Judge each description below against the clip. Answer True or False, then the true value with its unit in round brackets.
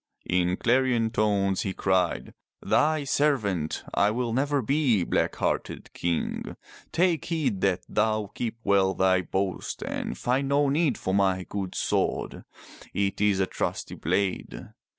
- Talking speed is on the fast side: False (140 wpm)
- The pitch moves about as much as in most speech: False (5.8 semitones)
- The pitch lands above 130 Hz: False (105 Hz)